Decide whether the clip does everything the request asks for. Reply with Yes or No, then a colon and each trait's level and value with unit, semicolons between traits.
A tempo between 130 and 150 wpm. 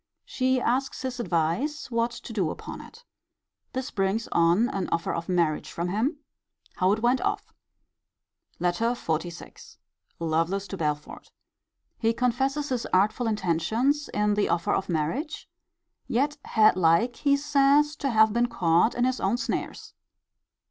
Yes: average, 145 wpm